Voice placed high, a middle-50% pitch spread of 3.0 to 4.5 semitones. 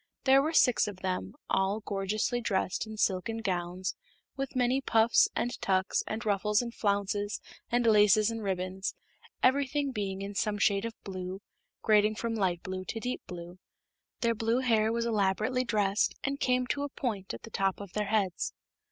Yes: high, 210 Hz; average, 3.4 semitones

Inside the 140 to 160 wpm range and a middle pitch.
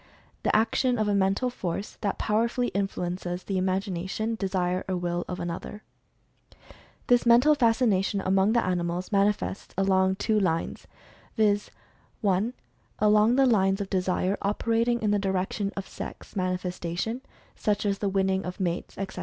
No: average, 155 wpm; high, 195 Hz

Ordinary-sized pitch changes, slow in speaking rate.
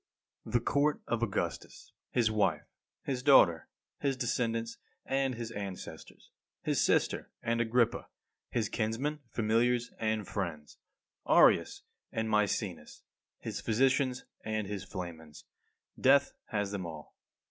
Yes: average, 3.6 semitones; slow, 120 wpm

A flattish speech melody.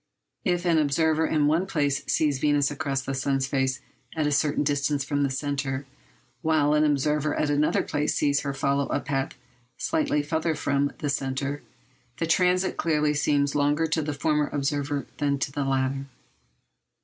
Yes: narrow, 1.6 semitones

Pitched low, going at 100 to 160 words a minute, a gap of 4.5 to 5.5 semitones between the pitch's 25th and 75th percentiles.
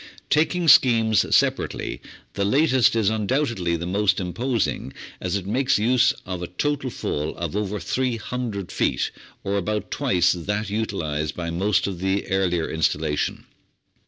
Yes: low, 100 Hz; average, 140 wpm; average, 4.9 semitones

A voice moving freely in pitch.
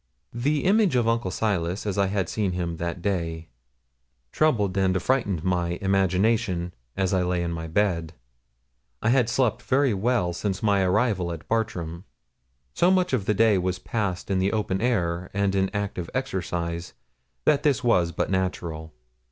No: average, 4.3 semitones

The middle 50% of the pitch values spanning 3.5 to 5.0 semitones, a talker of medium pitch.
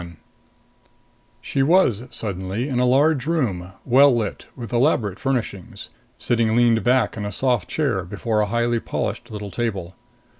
No: average, 4.0 semitones; low, 115 Hz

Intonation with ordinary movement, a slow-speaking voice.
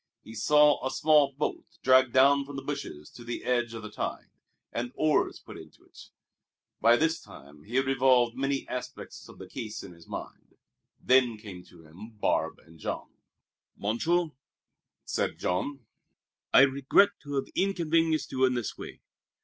No: average, 4.0 semitones; average, 165 wpm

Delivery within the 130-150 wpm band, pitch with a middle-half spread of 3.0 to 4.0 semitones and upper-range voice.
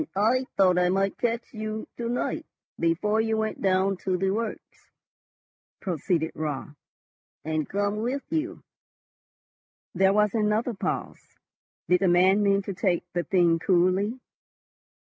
Yes: average, 140 wpm; average, 3.3 semitones; high, 195 Hz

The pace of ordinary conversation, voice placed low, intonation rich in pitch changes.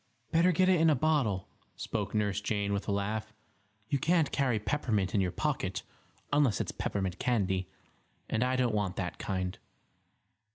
Yes: average, 165 wpm; low, 105 Hz; wide, 6.0 semitones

